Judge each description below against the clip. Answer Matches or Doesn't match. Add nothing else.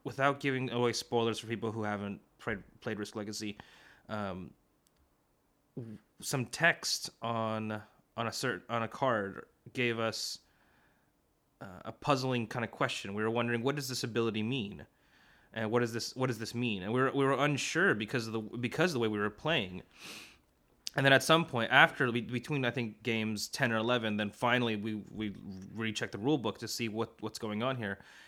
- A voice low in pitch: Matches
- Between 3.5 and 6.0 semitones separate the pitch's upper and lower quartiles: Doesn't match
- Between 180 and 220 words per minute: Matches